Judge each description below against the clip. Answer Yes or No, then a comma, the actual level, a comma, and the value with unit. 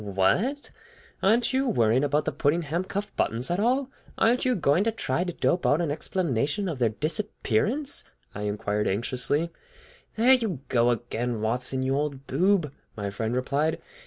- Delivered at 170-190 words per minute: No, average, 160 wpm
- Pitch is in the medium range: Yes, medium, 150 Hz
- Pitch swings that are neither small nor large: No, wide, 8.6 semitones